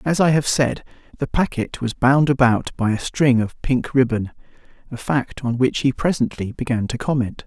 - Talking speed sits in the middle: Yes, average, 185 wpm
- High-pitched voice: No, low, 130 Hz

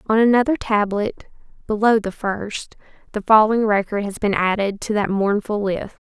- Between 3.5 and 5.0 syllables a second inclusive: Yes, 4.9 syllables/s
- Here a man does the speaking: No, female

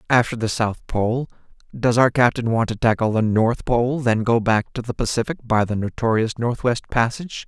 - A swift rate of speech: No, average, 195 wpm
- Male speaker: Yes, male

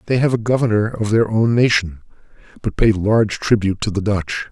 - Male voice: Yes, male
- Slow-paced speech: No, average, 200 wpm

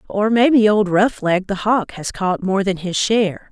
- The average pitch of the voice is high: Yes, high, 200 Hz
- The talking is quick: Yes, fast, 220 wpm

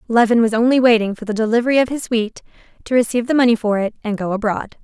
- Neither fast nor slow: No, fast, 235 wpm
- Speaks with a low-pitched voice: No, high, 230 Hz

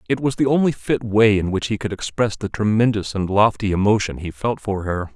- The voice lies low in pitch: Yes, low, 105 Hz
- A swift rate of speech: Yes, fast, 235 wpm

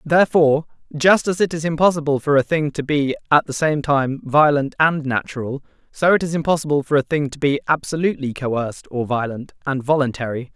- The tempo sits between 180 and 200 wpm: Yes, average, 190 wpm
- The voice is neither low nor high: Yes, medium, 145 Hz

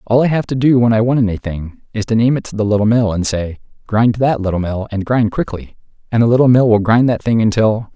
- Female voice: No, male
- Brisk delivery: Yes, fast, 265 wpm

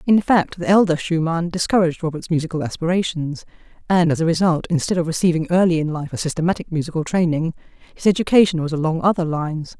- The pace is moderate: Yes, average, 180 wpm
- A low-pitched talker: No, medium, 165 Hz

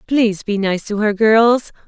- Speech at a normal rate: Yes, average, 190 wpm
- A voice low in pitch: No, high, 215 Hz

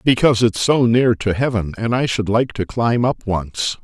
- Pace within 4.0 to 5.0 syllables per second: Yes, 4.7 syllables/s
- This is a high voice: No, low, 115 Hz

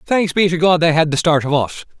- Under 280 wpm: No, fast, 300 wpm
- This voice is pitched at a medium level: Yes, medium, 165 Hz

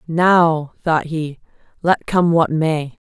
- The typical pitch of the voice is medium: Yes, medium, 160 Hz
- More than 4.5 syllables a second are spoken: No, 3.0 syllables/s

